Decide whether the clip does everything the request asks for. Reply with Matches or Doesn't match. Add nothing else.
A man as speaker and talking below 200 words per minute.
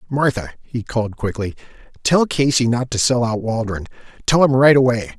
Matches